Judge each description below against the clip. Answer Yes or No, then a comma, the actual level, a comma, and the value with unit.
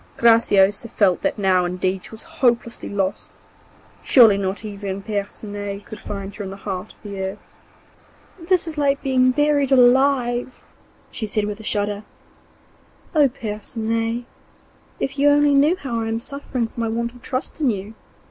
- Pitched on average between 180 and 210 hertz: No, high, 225 Hz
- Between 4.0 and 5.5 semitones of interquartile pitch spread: Yes, average, 4.6 semitones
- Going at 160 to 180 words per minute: Yes, average, 165 wpm